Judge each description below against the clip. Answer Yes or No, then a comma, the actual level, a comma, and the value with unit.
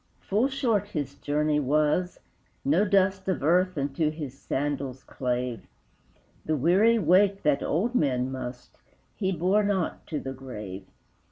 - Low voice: No, medium, 155 Hz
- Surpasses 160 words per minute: No, average, 140 wpm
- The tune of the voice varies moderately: No, wide, 6.0 semitones